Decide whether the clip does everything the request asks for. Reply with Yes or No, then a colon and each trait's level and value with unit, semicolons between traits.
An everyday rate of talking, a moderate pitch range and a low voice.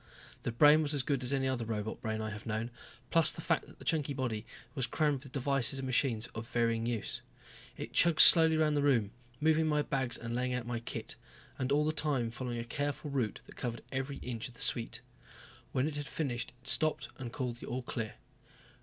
No: fast, 220 wpm; average, 3.7 semitones; low, 130 Hz